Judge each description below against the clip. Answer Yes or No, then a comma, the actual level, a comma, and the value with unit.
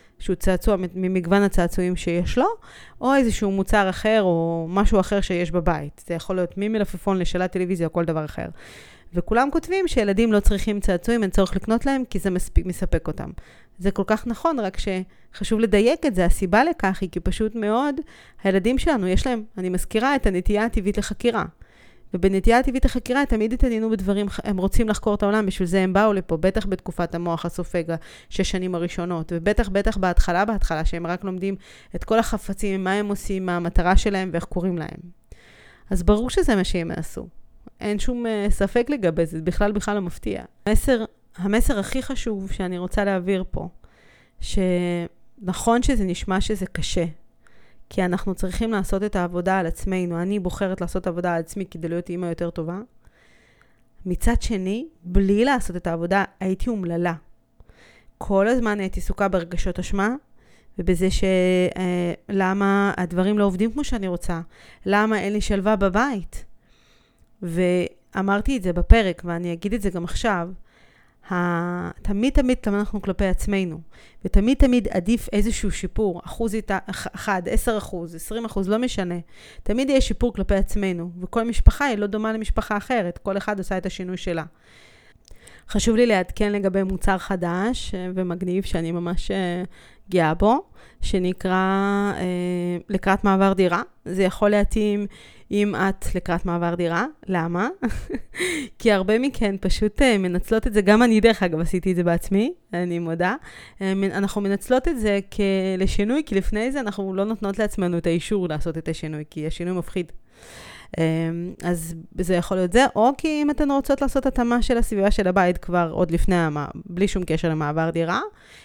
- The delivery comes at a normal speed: No, fast, 160 wpm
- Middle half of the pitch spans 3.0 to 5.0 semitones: Yes, average, 3.3 semitones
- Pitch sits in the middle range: No, high, 195 Hz